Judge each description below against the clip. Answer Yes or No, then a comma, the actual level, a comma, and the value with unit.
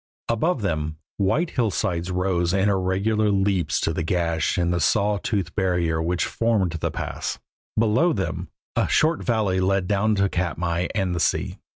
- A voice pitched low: Yes, very low, 95 Hz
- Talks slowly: No, average, 165 wpm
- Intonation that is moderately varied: Yes, average, 3.5 semitones